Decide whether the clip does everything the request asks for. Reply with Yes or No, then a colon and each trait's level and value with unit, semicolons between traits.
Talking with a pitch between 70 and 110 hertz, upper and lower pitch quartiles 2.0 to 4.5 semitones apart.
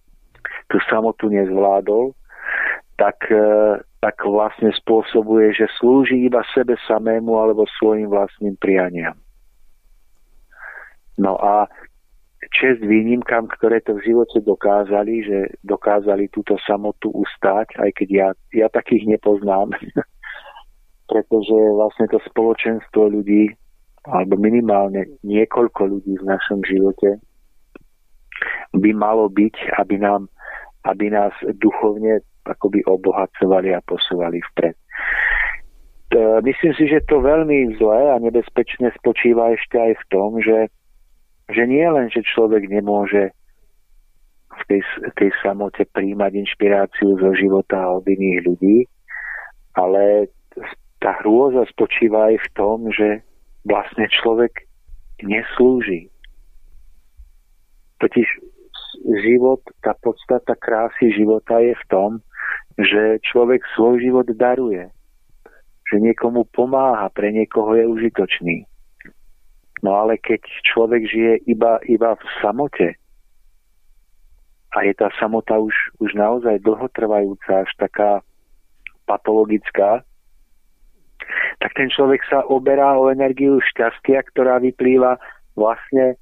Yes: low, 105 Hz; average, 2.8 semitones